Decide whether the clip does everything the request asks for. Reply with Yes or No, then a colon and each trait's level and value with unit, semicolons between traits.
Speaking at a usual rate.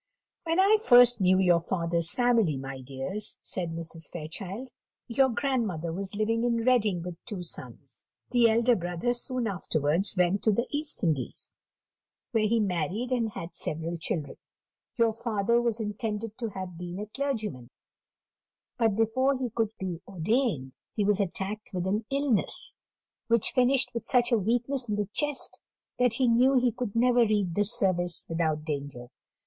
Yes: average, 160 wpm